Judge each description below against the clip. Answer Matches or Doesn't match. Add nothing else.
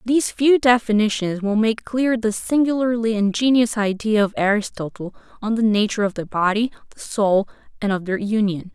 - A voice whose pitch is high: Matches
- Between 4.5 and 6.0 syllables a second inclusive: Matches